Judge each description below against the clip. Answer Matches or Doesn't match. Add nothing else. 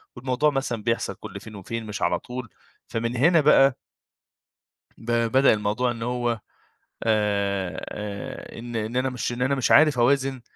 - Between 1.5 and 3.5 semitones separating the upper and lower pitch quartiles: Matches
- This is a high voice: Doesn't match